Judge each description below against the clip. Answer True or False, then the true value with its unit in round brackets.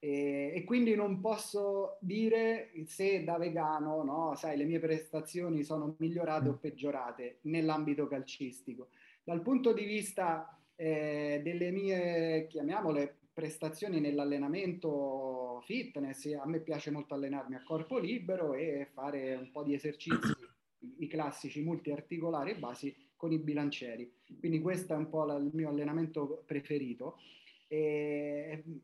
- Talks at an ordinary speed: True (130 wpm)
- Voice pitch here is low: False (155 Hz)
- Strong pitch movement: False (2.6 semitones)